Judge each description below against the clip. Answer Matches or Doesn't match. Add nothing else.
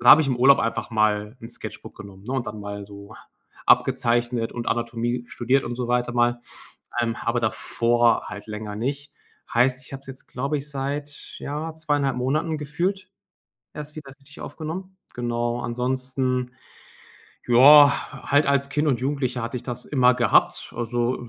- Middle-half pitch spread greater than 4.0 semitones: Doesn't match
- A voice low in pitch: Matches